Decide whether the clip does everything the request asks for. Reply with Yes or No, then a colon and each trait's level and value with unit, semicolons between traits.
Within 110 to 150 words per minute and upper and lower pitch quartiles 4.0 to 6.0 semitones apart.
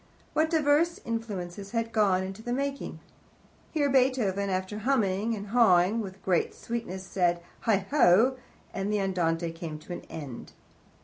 Yes: average, 140 wpm; average, 4.6 semitones